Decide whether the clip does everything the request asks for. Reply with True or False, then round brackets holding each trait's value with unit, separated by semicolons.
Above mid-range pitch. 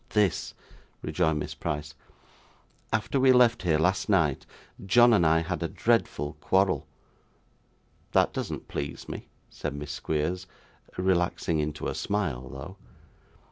False (90 Hz)